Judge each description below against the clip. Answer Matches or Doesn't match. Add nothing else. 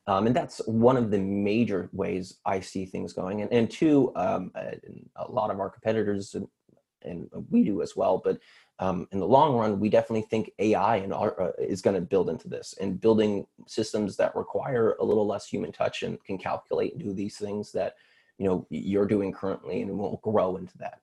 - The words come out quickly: Matches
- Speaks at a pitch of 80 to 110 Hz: Matches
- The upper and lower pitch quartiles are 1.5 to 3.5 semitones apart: Matches